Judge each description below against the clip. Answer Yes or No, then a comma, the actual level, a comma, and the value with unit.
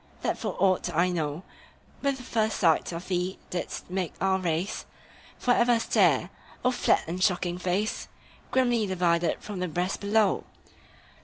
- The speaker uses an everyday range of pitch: Yes, average, 3.5 semitones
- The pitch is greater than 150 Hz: Yes, medium, 185 Hz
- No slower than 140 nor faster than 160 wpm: Yes, average, 155 wpm